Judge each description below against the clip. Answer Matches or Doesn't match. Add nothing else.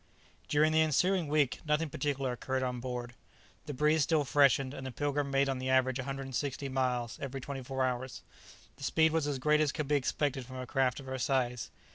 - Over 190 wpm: Matches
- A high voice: Doesn't match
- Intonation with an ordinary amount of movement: Doesn't match